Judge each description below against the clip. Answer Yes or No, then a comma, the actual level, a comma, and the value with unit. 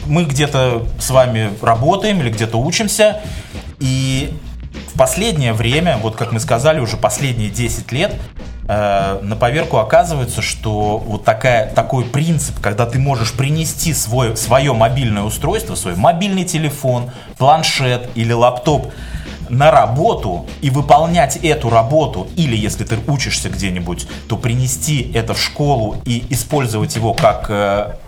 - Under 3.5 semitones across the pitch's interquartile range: No, average, 4.9 semitones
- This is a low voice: Yes, low, 120 Hz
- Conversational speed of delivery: Yes, average, 135 wpm